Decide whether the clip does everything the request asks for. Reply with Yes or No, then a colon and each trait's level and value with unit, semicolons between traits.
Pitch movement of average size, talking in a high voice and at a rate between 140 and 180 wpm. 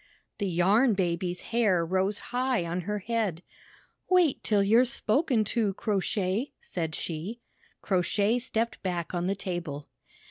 Yes: average, 4.5 semitones; high, 200 Hz; average, 145 wpm